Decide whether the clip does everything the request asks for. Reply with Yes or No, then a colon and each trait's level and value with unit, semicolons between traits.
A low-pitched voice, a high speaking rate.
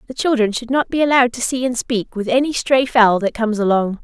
No: high, 240 Hz; fast, 255 wpm